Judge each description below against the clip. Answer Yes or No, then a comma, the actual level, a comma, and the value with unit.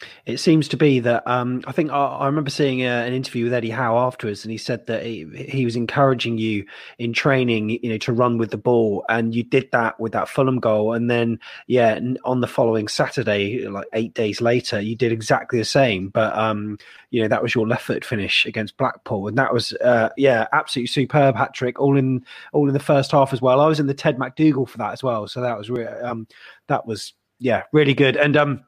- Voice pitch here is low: Yes, low, 125 Hz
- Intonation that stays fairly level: No, average, 3.2 semitones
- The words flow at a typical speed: No, fast, 235 wpm